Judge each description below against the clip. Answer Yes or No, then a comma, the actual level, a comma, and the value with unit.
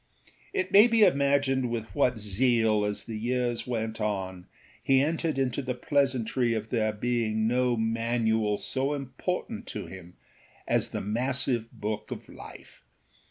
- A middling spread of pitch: Yes, average, 3.5 semitones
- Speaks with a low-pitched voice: Yes, low, 120 Hz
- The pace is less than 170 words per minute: Yes, average, 145 wpm